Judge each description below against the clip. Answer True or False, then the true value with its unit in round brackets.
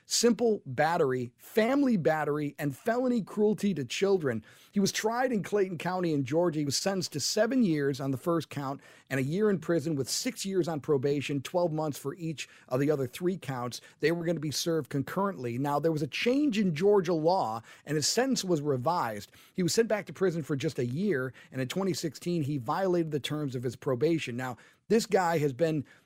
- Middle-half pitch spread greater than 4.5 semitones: True (5.5 semitones)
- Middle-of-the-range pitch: True (165 Hz)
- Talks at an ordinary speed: False (210 wpm)